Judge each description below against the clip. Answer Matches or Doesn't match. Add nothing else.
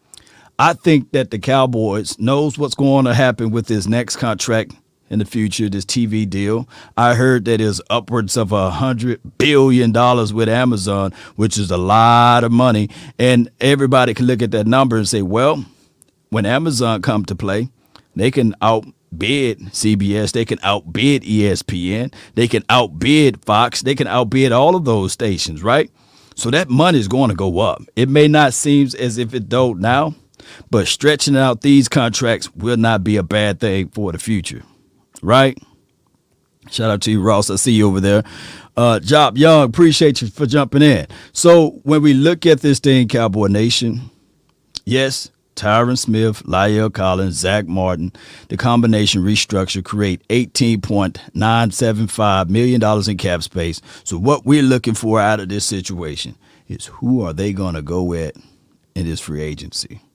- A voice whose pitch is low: Matches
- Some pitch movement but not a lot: Matches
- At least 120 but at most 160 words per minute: Doesn't match